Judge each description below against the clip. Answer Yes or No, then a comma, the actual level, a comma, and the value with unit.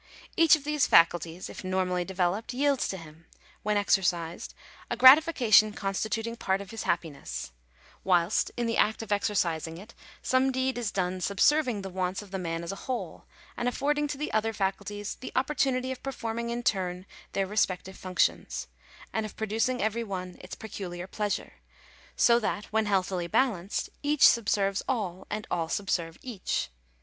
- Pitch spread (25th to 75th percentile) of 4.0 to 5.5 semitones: Yes, average, 4.6 semitones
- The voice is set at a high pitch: Yes, high, 205 Hz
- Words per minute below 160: No, average, 170 wpm